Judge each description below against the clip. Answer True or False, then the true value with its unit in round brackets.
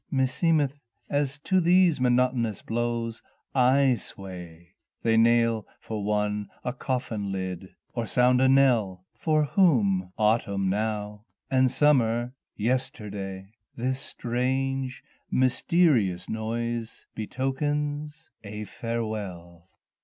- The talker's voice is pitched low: True (120 Hz)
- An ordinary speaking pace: False (100 wpm)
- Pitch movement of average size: True (4.2 semitones)